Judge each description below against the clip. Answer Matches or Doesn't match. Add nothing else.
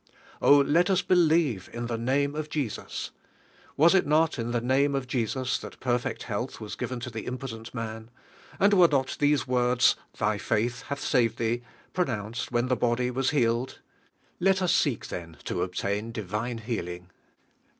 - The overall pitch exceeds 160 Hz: Doesn't match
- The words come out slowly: Doesn't match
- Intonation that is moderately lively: Matches